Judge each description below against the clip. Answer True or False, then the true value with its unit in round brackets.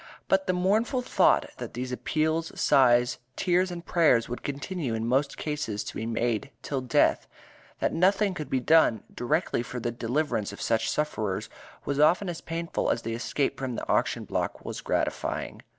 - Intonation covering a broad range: True (6.0 semitones)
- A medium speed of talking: True (175 wpm)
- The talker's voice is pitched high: False (140 Hz)